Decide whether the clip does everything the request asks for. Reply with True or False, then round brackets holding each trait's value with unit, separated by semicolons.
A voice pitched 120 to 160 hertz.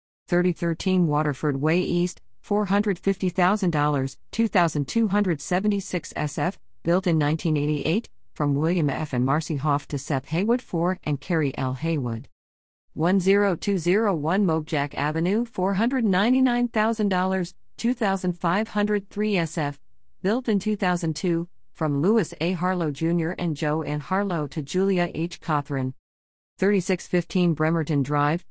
False (175 Hz)